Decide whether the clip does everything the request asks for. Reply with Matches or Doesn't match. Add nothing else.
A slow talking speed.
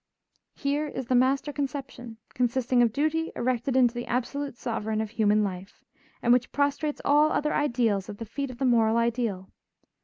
Doesn't match